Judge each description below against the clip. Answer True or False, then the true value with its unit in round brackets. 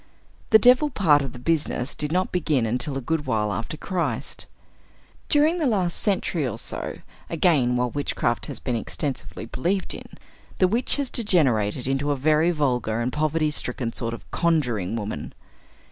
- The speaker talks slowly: False (165 wpm)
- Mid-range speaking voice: True (145 Hz)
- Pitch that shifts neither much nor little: False (6.2 semitones)